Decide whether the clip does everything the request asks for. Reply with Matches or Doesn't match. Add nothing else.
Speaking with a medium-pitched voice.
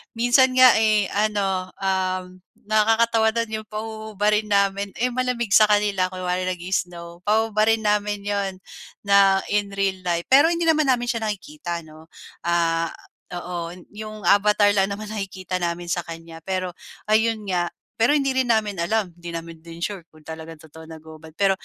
Doesn't match